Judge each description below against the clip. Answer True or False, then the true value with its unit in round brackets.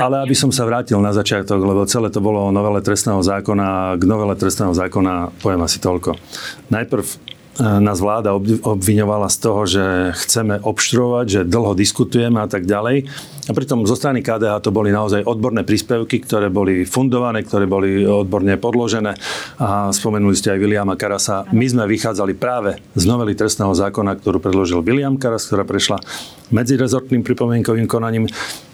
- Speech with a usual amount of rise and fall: True (3.0 semitones)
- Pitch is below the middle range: True (105 Hz)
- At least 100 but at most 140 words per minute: False (165 wpm)